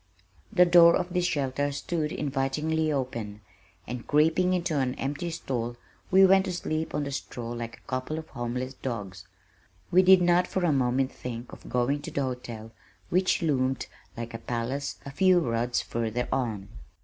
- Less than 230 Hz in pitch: Yes, low, 135 Hz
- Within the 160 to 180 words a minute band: Yes, average, 175 wpm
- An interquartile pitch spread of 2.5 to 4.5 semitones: No, wide, 5.6 semitones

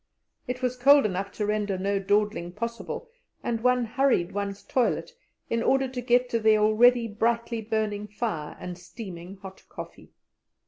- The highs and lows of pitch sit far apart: No, average, 3.4 semitones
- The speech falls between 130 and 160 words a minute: Yes, average, 155 wpm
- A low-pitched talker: No, high, 215 Hz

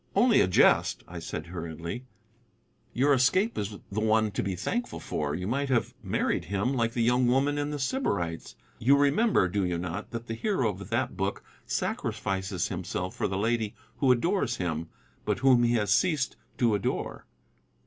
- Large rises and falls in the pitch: Yes, wide, 6.0 semitones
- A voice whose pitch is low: Yes, low, 115 Hz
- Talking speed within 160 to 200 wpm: Yes, average, 180 wpm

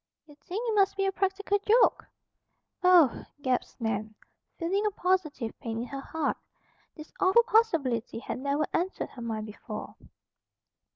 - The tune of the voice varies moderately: No, wide, 8.0 semitones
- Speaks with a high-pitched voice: Yes, very high, 330 Hz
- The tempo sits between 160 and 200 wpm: No, average, 150 wpm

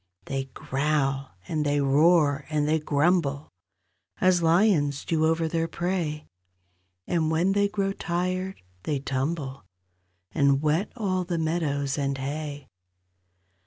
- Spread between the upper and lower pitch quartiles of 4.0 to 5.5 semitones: No, average, 3.5 semitones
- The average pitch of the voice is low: No, medium, 155 Hz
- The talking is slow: Yes, slow, 125 wpm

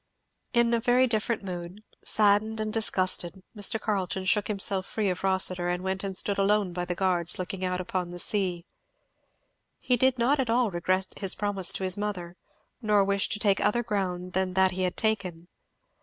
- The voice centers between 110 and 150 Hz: No, high, 195 Hz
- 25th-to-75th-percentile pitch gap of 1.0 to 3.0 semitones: Yes, average, 2.7 semitones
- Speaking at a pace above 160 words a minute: Yes, average, 185 wpm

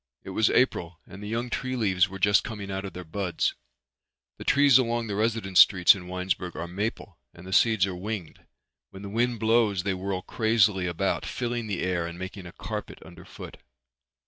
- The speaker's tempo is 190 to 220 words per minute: Yes, average, 195 wpm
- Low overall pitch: Yes, low, 100 Hz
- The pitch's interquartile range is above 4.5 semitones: No, average, 3.5 semitones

